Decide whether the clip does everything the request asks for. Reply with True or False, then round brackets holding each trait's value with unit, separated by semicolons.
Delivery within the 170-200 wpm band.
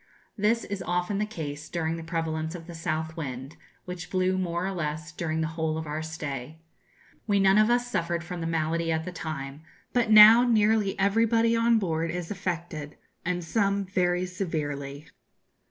True (175 wpm)